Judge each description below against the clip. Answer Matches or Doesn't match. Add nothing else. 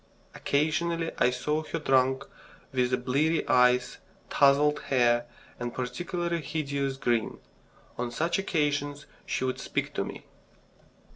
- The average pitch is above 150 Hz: Doesn't match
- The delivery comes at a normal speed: Doesn't match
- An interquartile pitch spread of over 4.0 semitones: Doesn't match